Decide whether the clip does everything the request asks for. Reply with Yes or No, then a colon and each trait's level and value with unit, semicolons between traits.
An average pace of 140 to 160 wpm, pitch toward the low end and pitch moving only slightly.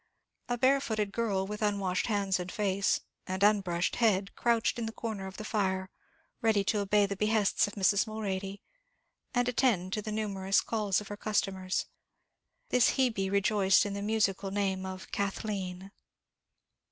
No: average, 155 wpm; high, 200 Hz; narrow, 2.1 semitones